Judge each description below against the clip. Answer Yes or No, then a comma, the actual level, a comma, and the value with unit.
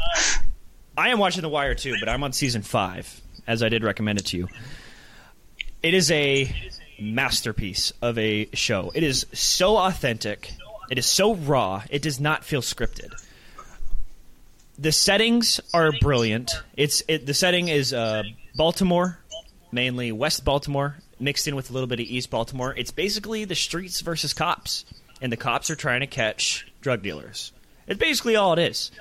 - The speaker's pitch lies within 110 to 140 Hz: Yes, low, 135 Hz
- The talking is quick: No, average, 170 wpm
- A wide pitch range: Yes, wide, 5.9 semitones